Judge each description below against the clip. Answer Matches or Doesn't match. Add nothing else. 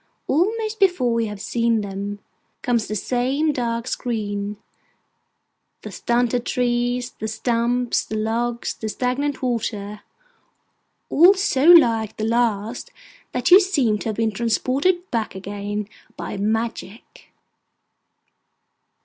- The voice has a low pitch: Doesn't match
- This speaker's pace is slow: Matches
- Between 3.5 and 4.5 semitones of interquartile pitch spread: Doesn't match